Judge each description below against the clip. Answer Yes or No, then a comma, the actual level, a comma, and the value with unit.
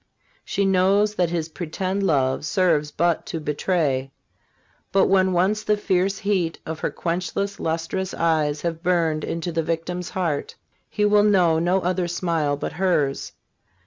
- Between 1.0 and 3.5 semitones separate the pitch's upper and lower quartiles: Yes, average, 2.9 semitones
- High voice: No, medium, 175 Hz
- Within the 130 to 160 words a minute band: Yes, average, 150 wpm